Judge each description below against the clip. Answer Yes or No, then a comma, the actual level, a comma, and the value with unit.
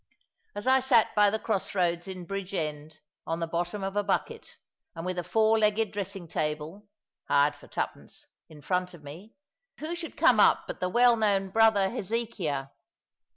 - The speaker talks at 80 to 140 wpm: No, average, 175 wpm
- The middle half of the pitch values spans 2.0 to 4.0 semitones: No, average, 4.4 semitones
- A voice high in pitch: Yes, high, 195 Hz